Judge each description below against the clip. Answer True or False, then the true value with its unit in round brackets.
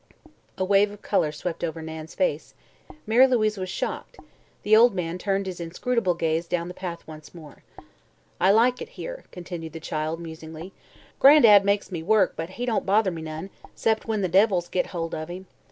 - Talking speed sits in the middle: True (190 wpm)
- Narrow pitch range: False (4.3 semitones)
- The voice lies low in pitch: False (185 Hz)